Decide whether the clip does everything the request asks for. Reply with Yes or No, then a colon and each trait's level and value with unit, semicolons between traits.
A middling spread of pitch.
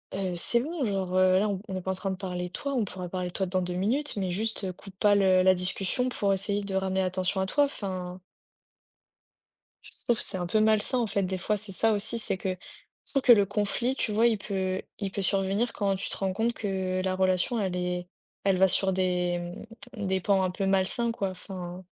No: narrow, 2.2 semitones